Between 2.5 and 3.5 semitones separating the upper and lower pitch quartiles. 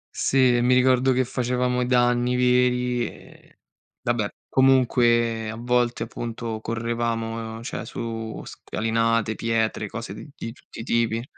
No: narrow, 1.6 semitones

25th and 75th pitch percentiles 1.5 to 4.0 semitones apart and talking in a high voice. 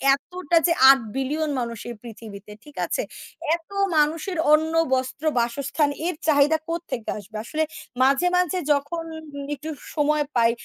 Yes: average, 3.7 semitones; very high, 295 Hz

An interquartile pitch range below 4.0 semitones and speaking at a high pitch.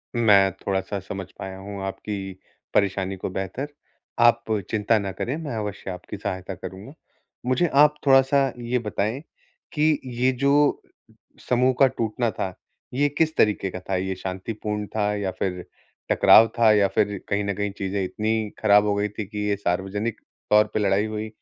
No: average, 3.5 semitones; low, 105 Hz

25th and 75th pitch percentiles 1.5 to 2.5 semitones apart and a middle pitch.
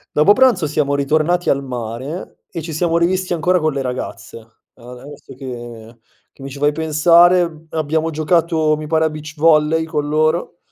No: average, 2.9 semitones; medium, 155 Hz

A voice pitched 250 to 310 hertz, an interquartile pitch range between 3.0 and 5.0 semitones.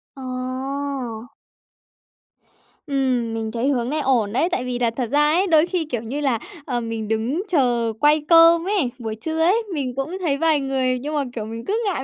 Yes: very high, 265 Hz; average, 4.5 semitones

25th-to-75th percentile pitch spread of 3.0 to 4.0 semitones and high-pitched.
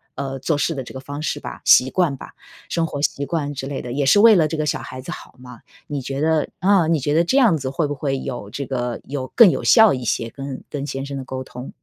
No: average, 3.4 semitones; medium, 140 Hz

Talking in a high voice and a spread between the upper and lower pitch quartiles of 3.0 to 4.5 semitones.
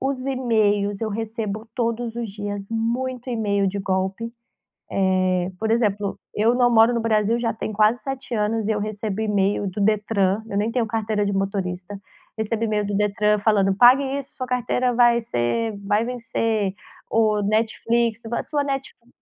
No: high, 220 Hz; narrow, 2.5 semitones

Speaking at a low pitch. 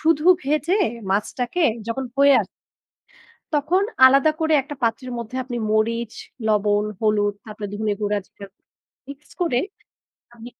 No: high, 240 Hz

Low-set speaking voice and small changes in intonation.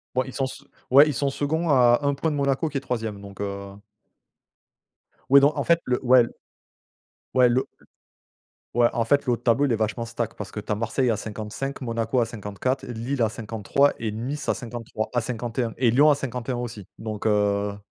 No: low, 120 Hz; average, 3.5 semitones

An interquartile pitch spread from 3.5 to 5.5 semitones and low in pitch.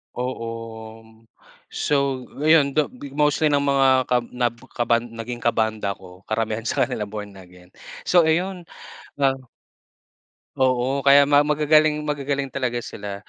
Yes: average, 4.5 semitones; low, 130 Hz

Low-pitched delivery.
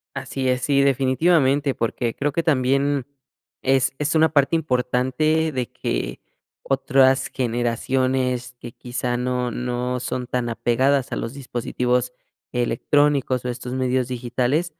Yes: low, 130 Hz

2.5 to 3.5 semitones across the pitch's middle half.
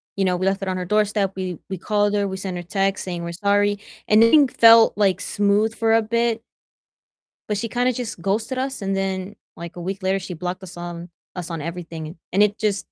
Yes: average, 2.8 semitones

